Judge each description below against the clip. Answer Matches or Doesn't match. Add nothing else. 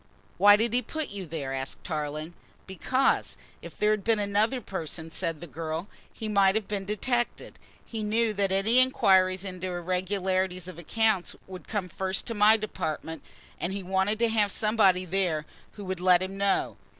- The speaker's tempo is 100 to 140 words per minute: Doesn't match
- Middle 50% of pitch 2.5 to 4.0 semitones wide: Matches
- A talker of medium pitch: Doesn't match